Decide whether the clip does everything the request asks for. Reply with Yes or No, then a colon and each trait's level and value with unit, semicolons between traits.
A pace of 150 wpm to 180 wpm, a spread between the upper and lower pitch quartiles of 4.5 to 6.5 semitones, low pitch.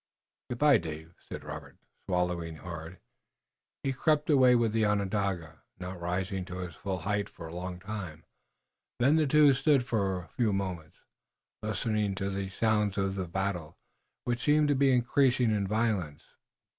Yes: average, 160 wpm; average, 5.2 semitones; low, 100 Hz